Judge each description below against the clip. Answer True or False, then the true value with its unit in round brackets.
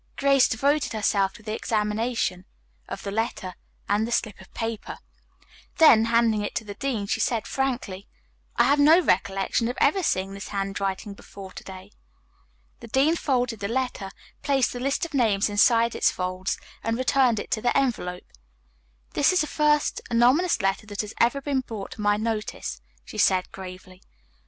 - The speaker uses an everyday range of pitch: True (4.7 semitones)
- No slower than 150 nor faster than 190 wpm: True (175 wpm)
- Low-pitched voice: False (225 Hz)